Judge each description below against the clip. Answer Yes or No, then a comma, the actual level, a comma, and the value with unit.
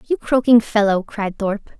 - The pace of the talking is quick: No, average, 165 wpm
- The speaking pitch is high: Yes, high, 220 Hz